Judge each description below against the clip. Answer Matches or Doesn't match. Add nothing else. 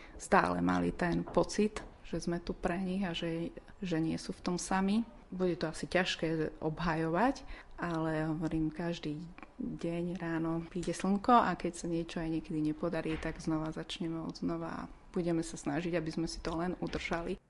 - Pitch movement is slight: Matches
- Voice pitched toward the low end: Doesn't match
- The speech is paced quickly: Matches